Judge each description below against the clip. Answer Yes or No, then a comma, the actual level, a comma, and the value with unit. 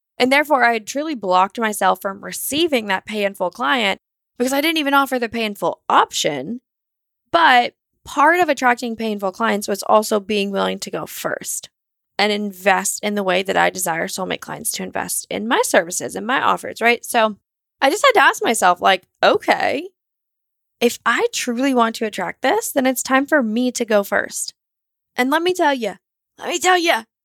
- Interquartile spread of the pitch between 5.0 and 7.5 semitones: Yes, wide, 5.4 semitones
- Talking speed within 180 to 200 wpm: Yes, average, 185 wpm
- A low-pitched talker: No, high, 235 Hz